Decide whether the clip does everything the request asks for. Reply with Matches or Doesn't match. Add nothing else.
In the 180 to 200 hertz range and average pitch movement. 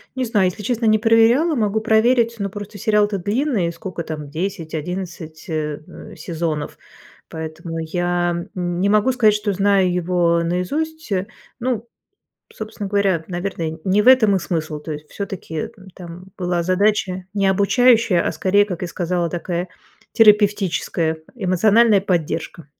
Matches